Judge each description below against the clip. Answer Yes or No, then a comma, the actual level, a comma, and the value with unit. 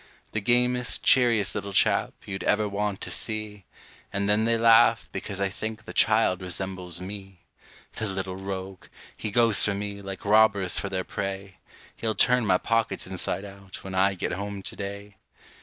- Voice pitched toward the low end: Yes, low, 100 Hz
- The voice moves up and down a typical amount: No, narrow, 2.1 semitones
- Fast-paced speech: No, average, 175 wpm